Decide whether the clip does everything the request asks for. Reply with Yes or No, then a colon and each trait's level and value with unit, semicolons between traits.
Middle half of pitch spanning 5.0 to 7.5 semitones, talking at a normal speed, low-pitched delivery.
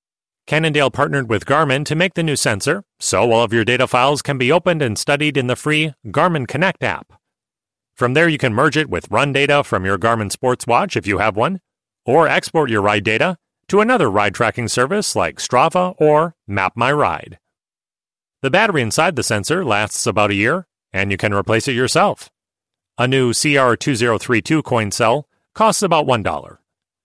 Yes: wide, 5.5 semitones; average, 185 wpm; low, 130 Hz